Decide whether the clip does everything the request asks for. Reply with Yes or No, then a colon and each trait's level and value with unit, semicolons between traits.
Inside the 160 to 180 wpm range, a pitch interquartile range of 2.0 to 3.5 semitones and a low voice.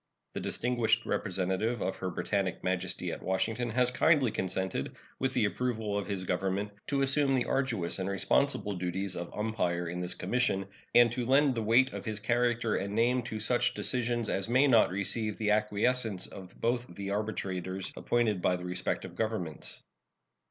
No: average, 170 wpm; average, 4.3 semitones; low, 110 Hz